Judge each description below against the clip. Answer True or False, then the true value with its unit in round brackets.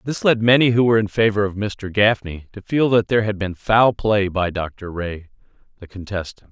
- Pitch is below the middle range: True (105 Hz)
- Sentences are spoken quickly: True (210 wpm)